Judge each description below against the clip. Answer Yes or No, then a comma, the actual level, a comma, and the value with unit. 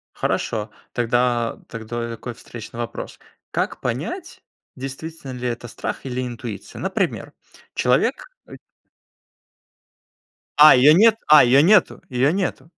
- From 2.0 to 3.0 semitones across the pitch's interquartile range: No, average, 3.9 semitones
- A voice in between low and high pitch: No, low, 125 Hz